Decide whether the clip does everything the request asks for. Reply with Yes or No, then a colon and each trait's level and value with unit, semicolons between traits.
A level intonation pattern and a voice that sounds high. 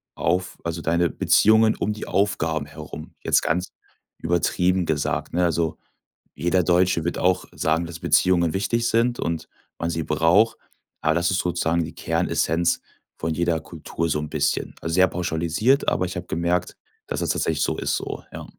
No: narrow, 2.1 semitones; very low, 85 Hz